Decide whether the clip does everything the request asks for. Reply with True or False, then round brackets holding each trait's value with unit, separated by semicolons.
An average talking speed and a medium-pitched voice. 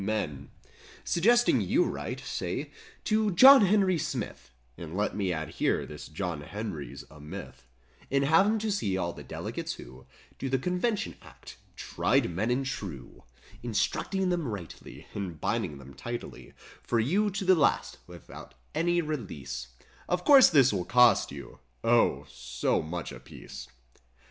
False (155 wpm; 120 Hz)